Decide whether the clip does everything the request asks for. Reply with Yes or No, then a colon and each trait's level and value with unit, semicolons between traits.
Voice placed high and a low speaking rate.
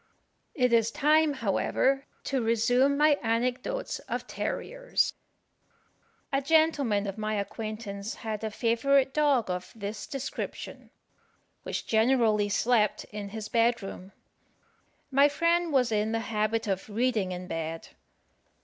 Yes: high, 230 Hz; slow, 125 wpm